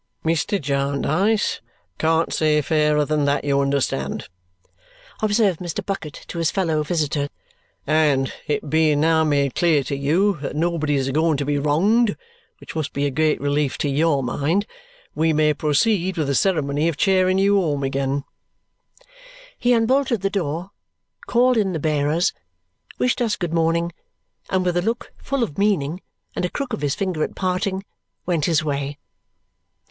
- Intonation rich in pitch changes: No, average, 4.6 semitones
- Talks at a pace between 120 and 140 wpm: No, average, 160 wpm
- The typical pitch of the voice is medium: Yes, medium, 160 Hz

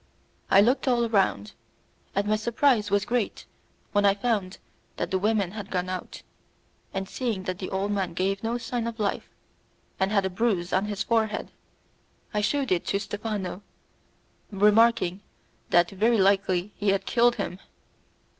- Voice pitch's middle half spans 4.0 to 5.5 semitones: No, average, 2.8 semitones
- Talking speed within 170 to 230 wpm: No, average, 160 wpm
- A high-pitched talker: Yes, high, 205 Hz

